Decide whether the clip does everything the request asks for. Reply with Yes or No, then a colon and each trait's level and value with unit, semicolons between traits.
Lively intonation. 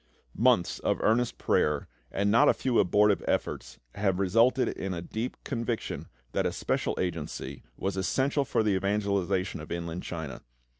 No: average, 4.6 semitones